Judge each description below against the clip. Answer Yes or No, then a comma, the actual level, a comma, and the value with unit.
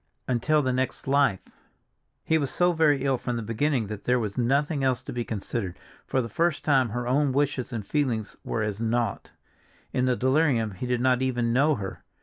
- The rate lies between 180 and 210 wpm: Yes, average, 200 wpm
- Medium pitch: No, low, 125 Hz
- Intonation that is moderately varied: Yes, average, 3.4 semitones